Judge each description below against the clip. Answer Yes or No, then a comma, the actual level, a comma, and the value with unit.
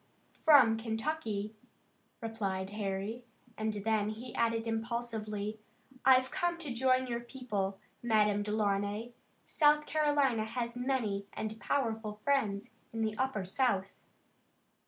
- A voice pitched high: Yes, high, 225 Hz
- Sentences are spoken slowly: Yes, slow, 115 wpm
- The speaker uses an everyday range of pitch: Yes, average, 3.5 semitones